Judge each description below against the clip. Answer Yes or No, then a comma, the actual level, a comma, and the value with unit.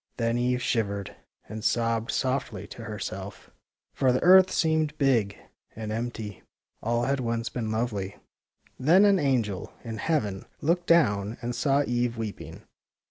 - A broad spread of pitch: No, average, 4.1 semitones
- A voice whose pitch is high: No, low, 120 Hz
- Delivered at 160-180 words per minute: No, average, 145 wpm